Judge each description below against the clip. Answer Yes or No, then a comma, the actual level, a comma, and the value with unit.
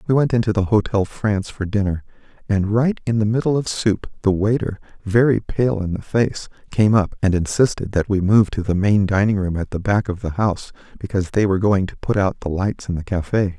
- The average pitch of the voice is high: No, low, 100 Hz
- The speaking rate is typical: No, fast, 230 wpm